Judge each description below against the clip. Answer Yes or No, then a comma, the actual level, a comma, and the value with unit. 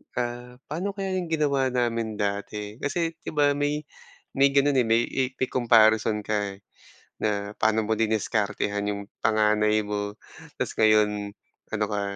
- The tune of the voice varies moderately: Yes, average, 4.1 semitones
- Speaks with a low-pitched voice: Yes, low, 110 Hz